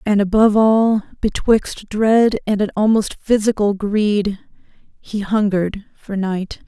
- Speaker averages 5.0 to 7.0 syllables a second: No, 4.2 syllables/s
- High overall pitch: Yes, high, 210 Hz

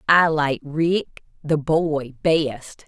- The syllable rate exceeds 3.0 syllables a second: No, 2.6 syllables/s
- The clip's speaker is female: Yes, female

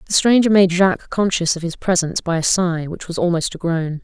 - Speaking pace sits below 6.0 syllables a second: Yes, 5.7 syllables/s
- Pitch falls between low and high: Yes, medium, 175 Hz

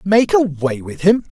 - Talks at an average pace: Yes, average, 175 wpm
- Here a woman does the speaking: No, male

